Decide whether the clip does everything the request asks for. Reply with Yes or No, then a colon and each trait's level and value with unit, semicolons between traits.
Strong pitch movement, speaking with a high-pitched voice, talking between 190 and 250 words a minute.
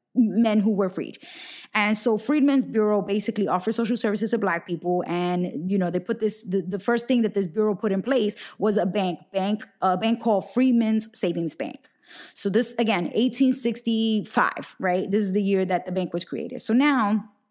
No: average, 3.2 semitones; high, 215 Hz; average, 195 wpm